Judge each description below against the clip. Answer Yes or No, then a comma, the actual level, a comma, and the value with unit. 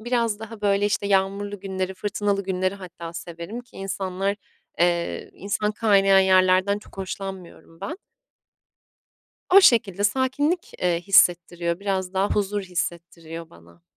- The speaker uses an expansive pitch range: No, narrow, 2.4 semitones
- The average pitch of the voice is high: Yes, high, 195 Hz